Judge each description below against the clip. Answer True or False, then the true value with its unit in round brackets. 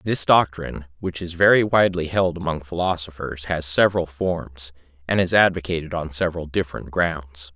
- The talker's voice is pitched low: True (85 Hz)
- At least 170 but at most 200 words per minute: False (150 wpm)